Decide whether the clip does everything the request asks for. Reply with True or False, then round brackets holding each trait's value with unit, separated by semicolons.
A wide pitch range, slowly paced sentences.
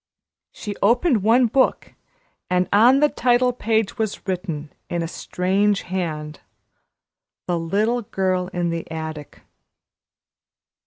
False (4.9 semitones; 115 wpm)